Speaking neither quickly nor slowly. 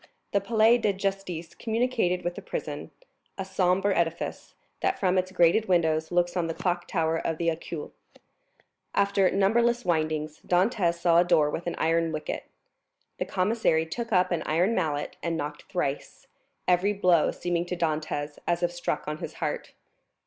Yes: average, 165 wpm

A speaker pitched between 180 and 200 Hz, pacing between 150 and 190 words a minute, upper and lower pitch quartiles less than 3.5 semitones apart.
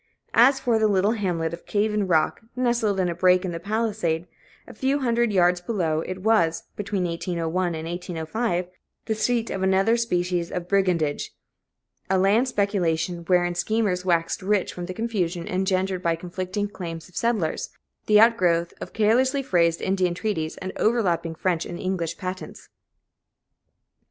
No: medium, 185 Hz; average, 155 wpm; average, 3.8 semitones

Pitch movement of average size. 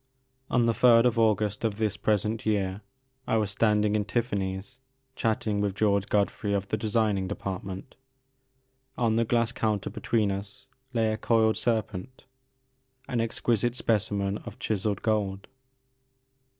No: narrow, 2.2 semitones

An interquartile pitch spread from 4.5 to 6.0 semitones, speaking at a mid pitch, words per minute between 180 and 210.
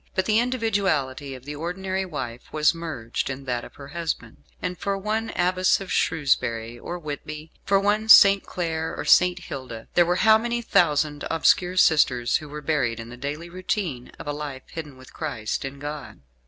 Yes: average, 5.3 semitones; medium, 155 Hz; average, 185 wpm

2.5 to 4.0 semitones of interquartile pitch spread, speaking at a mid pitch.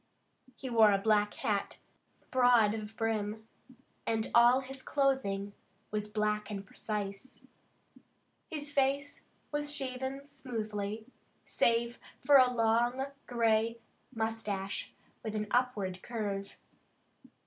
No: average, 3.6 semitones; high, 225 Hz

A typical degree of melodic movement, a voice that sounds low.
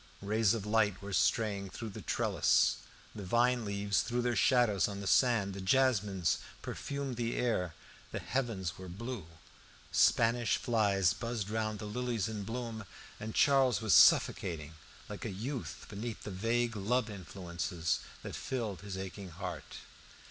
Yes: average, 3.5 semitones; low, 105 Hz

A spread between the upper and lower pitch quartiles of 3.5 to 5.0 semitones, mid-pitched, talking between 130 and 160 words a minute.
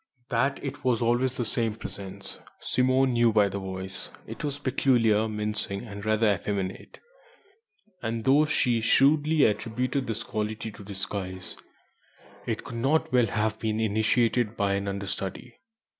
No: average, 3.8 semitones; low, 110 Hz; average, 145 wpm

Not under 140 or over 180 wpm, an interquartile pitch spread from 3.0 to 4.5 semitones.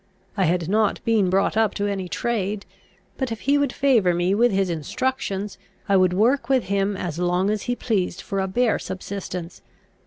No: average, 190 wpm; average, 3.6 semitones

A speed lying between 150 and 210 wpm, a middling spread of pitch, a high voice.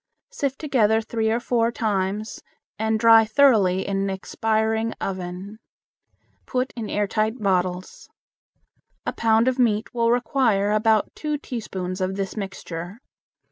No: slow, 135 wpm; average, 3.0 semitones; high, 220 Hz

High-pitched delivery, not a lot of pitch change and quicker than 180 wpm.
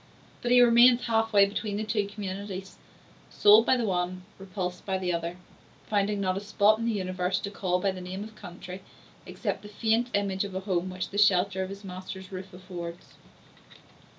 Yes: high, 195 Hz; narrow, 2.3 semitones; average, 195 wpm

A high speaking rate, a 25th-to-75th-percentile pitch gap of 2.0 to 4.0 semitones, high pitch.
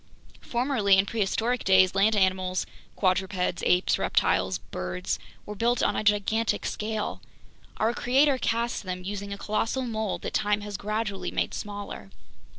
No: average, 145 wpm; average, 2.9 semitones; high, 205 Hz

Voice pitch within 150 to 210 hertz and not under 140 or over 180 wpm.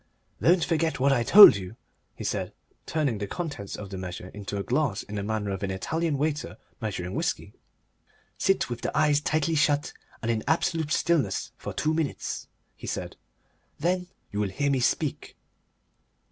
No: medium, 140 Hz; average, 175 wpm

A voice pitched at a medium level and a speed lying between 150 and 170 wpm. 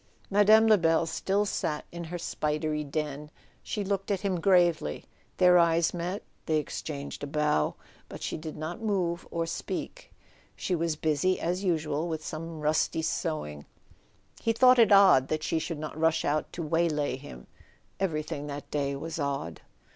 Yes: medium, 160 Hz; average, 160 wpm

